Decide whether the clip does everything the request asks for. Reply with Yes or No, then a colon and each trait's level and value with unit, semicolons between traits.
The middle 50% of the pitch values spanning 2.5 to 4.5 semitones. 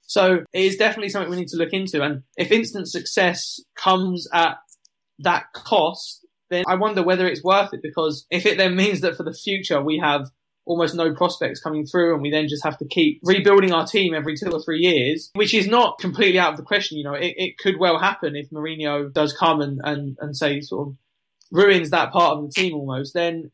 Yes: average, 3.8 semitones